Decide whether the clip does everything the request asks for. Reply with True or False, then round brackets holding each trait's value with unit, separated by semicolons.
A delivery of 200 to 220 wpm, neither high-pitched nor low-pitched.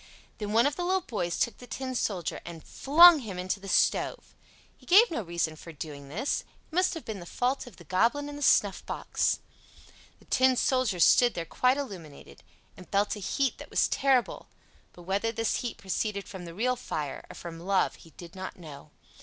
False (205 wpm; 210 Hz)